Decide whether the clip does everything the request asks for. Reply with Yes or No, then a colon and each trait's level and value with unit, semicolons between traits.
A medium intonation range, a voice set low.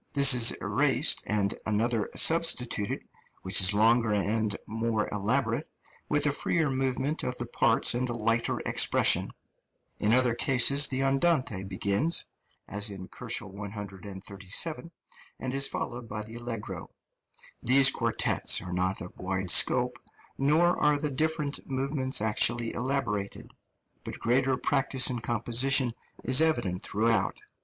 Yes: average, 4.6 semitones; low, 120 Hz